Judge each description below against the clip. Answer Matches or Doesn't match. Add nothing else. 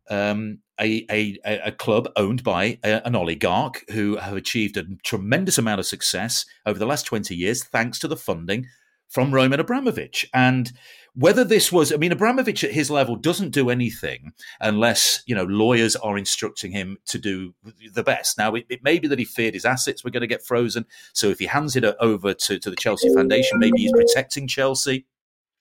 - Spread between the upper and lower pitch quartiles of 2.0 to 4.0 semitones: Doesn't match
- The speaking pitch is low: Matches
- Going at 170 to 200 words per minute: Matches